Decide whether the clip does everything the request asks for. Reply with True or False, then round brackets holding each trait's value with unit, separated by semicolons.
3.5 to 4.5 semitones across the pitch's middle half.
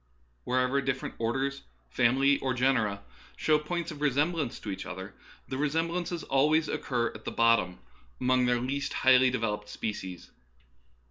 True (3.8 semitones)